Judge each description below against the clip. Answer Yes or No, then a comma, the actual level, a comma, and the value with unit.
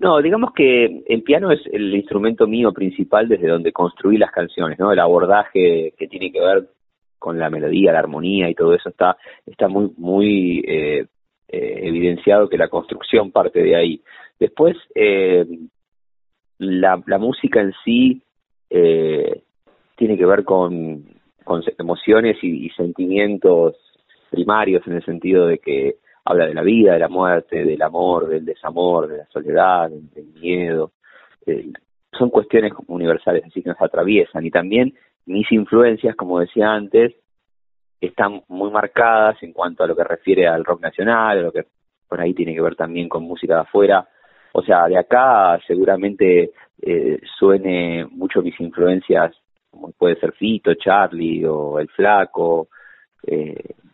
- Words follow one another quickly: No, average, 160 wpm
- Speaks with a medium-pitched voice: No, low, 105 Hz